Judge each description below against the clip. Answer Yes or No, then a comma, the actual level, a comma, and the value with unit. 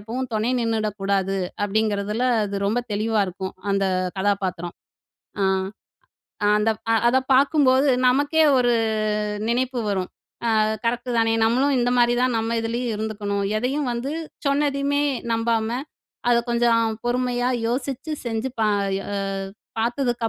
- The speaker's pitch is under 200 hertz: No, high, 230 Hz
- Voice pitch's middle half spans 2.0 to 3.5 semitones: Yes, average, 3.2 semitones